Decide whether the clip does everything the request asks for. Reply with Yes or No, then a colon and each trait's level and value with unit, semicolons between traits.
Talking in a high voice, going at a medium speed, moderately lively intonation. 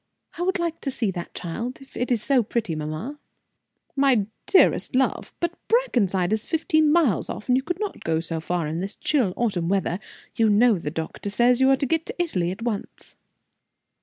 No: high, 235 Hz; average, 195 wpm; wide, 7.4 semitones